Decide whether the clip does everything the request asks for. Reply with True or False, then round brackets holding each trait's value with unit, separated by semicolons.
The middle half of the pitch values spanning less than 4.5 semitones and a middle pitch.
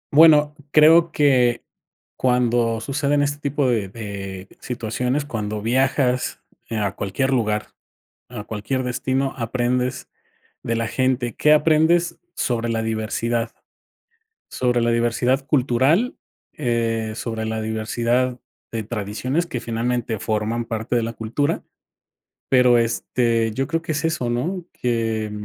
False (3.1 semitones; 120 Hz)